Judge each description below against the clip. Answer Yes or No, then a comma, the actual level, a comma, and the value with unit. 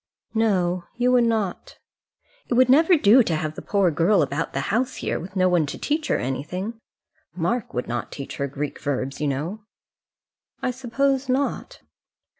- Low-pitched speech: No, high, 195 Hz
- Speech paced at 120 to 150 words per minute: No, average, 175 wpm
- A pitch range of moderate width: No, wide, 8.2 semitones